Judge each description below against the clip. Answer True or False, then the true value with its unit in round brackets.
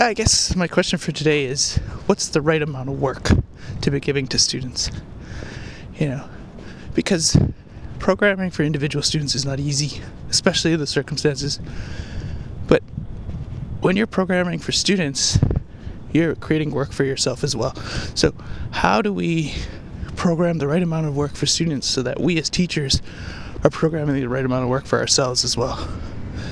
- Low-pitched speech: False (145 Hz)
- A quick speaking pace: False (165 wpm)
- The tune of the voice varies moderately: True (4.8 semitones)